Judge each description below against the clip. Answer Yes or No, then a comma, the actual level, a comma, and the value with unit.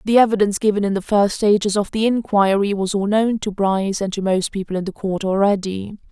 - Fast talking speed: Yes, fast, 225 wpm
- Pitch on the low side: No, high, 200 Hz